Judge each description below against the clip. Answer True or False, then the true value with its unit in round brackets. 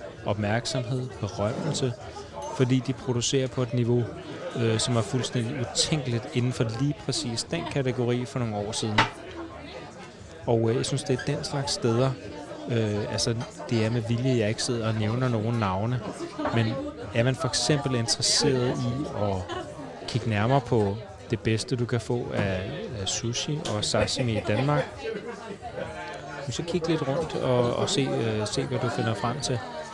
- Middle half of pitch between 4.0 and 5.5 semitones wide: False (2.9 semitones)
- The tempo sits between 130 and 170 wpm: True (160 wpm)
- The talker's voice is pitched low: True (120 Hz)